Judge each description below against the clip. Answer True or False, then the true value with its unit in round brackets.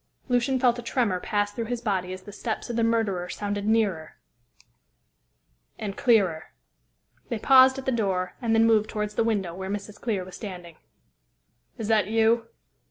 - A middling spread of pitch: True (3.3 semitones)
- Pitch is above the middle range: True (215 Hz)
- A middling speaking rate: True (170 wpm)